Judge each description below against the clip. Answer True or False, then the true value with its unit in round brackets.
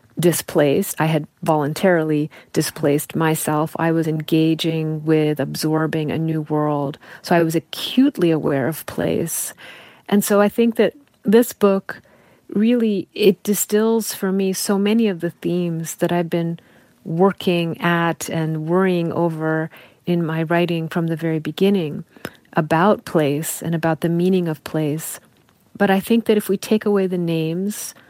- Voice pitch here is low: False (170 Hz)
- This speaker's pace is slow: False (150 wpm)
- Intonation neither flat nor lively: True (3.6 semitones)